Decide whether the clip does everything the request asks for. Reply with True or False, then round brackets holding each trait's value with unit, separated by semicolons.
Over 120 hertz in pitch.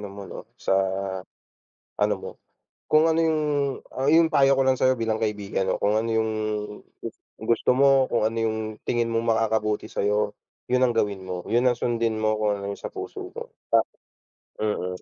False (110 Hz)